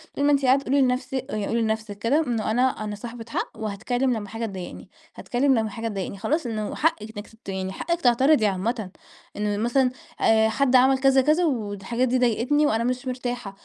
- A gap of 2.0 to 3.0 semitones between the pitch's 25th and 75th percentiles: No, average, 3.5 semitones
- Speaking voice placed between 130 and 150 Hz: No, high, 235 Hz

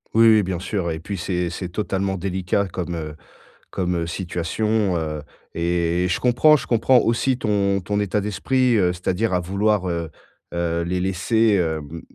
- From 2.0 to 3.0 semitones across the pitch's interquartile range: No, average, 3.6 semitones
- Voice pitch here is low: Yes, very low, 95 Hz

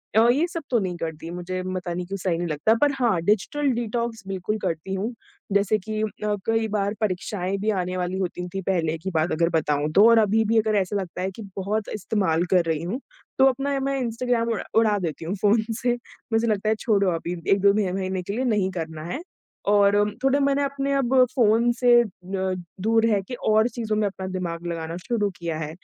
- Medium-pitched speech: No, high, 200 Hz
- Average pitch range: Yes, average, 4.1 semitones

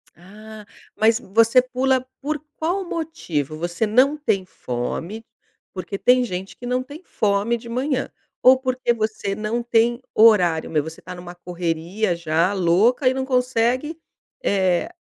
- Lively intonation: Yes, wide, 5.9 semitones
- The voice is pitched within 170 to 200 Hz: No, high, 220 Hz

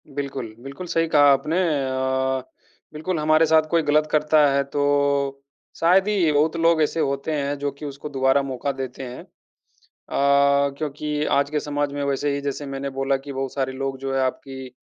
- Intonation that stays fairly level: Yes, narrow, 2.2 semitones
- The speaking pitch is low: No, medium, 145 Hz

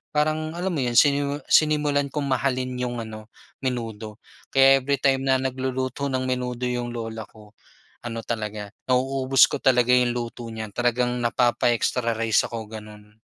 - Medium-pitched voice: No, low, 125 Hz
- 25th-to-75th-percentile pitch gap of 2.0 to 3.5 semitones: Yes, average, 2.7 semitones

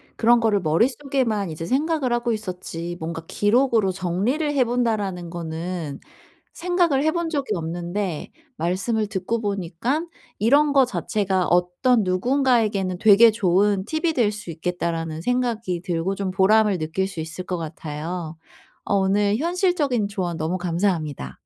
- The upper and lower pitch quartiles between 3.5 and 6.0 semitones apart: Yes, wide, 5.6 semitones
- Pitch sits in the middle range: No, high, 200 Hz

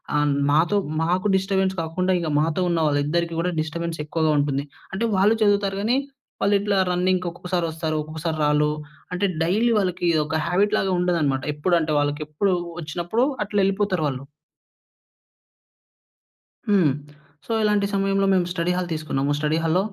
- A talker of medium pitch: Yes, medium, 175 Hz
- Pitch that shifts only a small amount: No, average, 3.8 semitones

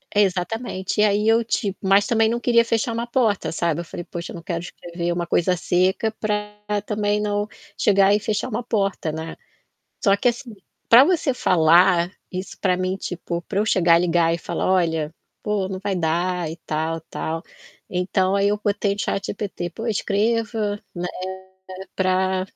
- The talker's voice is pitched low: No, high, 195 Hz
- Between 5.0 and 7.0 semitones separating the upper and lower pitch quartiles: No, average, 3.3 semitones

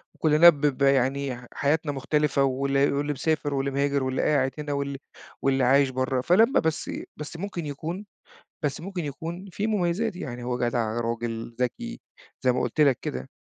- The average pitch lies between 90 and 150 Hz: Yes, medium, 140 Hz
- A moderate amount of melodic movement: Yes, average, 3.4 semitones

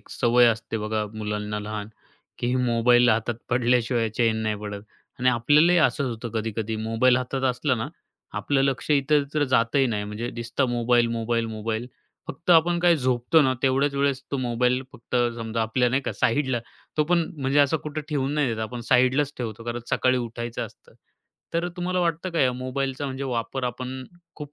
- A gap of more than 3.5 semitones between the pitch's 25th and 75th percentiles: No, average, 3.2 semitones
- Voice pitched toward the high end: No, low, 125 Hz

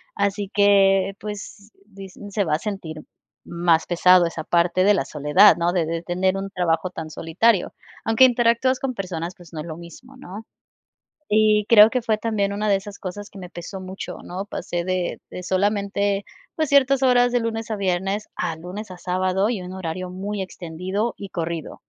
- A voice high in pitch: Yes, high, 195 Hz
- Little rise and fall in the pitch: No, average, 3.0 semitones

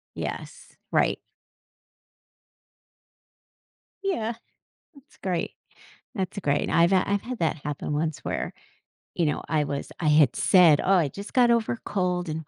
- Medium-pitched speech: Yes, medium, 180 Hz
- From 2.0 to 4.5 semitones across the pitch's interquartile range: No, average, 4.9 semitones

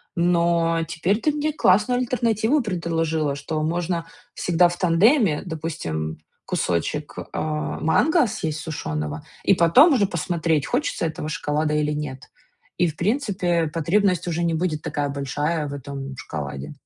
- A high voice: No, medium, 165 Hz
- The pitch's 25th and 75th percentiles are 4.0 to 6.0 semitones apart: No, average, 3.6 semitones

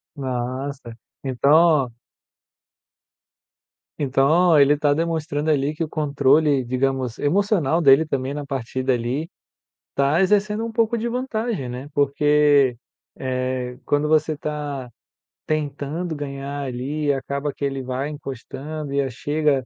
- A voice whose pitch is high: No, medium, 145 Hz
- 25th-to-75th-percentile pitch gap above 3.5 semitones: No, narrow, 2.6 semitones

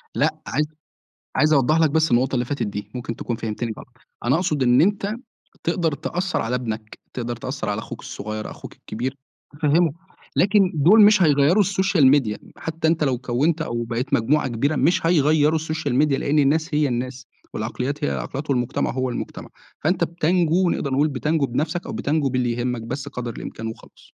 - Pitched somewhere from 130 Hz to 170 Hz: Yes, medium, 140 Hz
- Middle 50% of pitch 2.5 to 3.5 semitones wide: No, average, 4.7 semitones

